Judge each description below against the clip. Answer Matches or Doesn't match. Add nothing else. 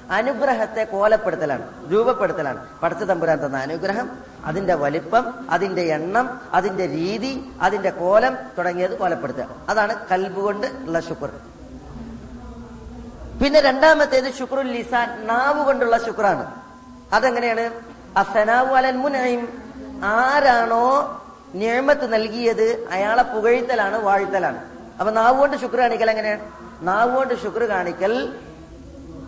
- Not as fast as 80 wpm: Doesn't match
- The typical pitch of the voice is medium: Doesn't match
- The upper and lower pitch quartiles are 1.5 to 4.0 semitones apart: Doesn't match